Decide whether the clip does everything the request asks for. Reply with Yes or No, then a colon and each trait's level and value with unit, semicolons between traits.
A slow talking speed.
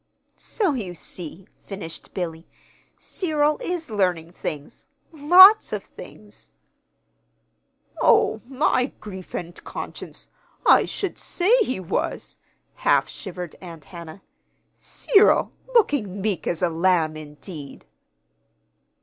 Yes: slow, 105 wpm